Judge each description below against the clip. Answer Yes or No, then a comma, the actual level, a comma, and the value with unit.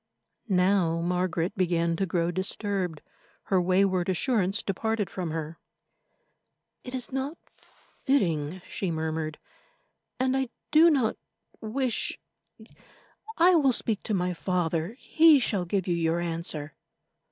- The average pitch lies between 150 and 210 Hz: Yes, medium, 185 Hz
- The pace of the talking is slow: Yes, slow, 120 wpm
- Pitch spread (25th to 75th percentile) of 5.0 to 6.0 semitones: Yes, wide, 5.4 semitones